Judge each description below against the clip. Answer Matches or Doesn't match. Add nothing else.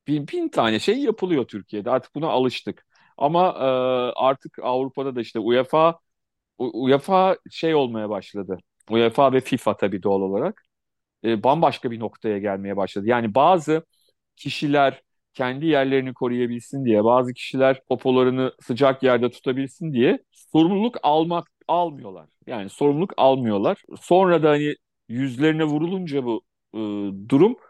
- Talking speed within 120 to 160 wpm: Matches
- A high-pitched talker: Doesn't match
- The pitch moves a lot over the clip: Doesn't match